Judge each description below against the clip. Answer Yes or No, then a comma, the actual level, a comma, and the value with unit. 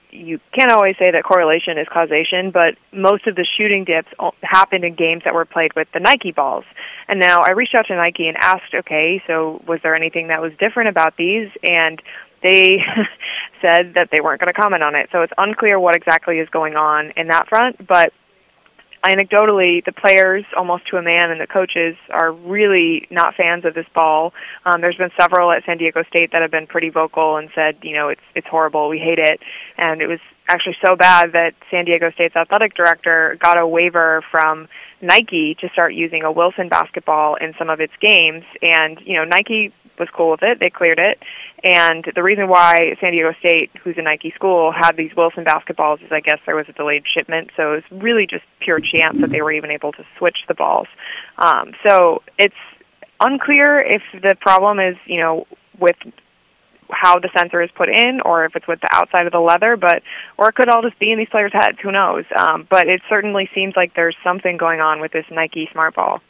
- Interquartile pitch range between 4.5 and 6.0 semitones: No, average, 2.7 semitones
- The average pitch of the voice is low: No, medium, 170 Hz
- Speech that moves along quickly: Yes, fast, 215 wpm